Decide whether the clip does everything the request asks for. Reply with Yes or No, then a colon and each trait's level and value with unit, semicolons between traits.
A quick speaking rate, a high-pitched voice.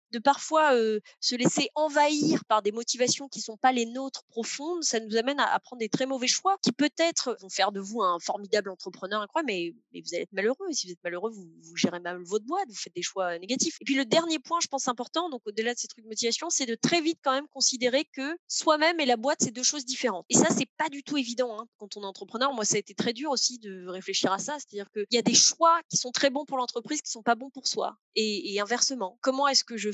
Yes: fast, 280 wpm; very high, 250 Hz